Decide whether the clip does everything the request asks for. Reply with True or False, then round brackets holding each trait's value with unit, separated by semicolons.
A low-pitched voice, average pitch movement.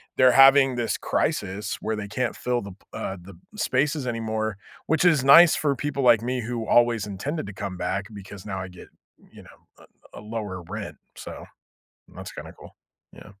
True (115 Hz; 4.3 semitones)